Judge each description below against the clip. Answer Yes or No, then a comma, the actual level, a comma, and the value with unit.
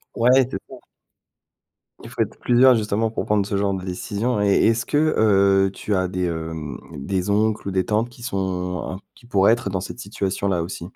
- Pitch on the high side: No, low, 100 Hz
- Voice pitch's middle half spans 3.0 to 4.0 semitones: Yes, average, 3.3 semitones